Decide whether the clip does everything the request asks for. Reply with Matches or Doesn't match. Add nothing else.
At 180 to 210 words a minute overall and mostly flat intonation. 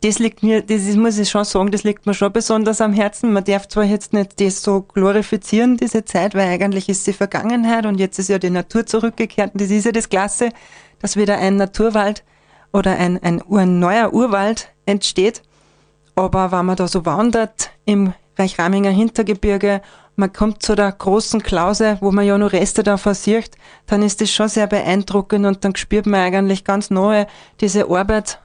Matches